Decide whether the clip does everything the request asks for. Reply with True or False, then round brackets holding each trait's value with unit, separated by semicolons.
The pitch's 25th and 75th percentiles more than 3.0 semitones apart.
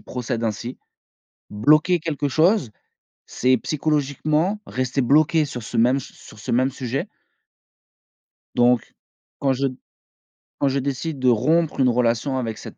True (3.7 semitones)